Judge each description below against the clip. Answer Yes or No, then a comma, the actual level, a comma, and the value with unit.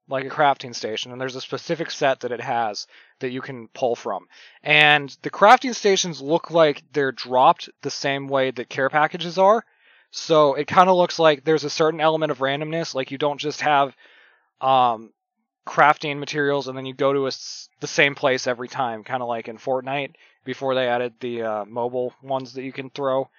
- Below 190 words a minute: No, fast, 205 wpm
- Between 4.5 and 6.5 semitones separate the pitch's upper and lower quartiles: No, average, 2.8 semitones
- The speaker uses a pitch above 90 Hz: Yes, low, 135 Hz